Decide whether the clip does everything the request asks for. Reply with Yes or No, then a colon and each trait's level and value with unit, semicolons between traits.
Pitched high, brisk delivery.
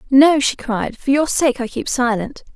Yes: very high, 260 Hz; fast, 210 wpm